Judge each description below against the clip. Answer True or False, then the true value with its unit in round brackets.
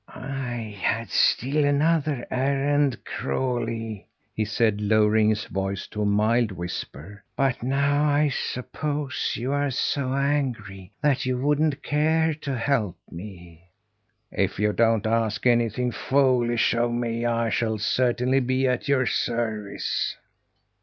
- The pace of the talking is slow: True (130 wpm)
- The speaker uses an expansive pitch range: False (4.2 semitones)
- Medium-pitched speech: False (120 Hz)